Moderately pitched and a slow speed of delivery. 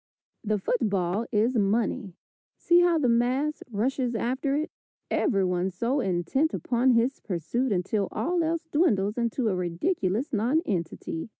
No: high, 235 Hz; slow, 130 wpm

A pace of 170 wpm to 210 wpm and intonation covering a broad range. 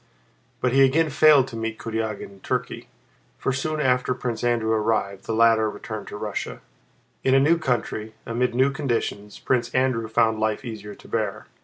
No: average, 175 wpm; average, 3.2 semitones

